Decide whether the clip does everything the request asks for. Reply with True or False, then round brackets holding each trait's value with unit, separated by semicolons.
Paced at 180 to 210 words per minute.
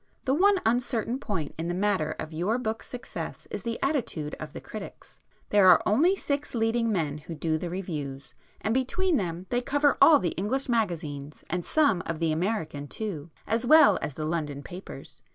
True (190 wpm)